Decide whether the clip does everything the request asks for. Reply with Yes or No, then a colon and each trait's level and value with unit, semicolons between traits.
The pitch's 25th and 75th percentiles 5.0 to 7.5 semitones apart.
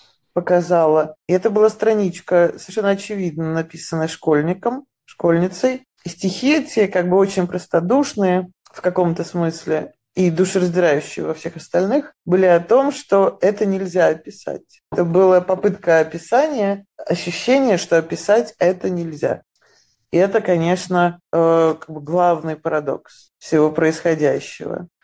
No: average, 3.0 semitones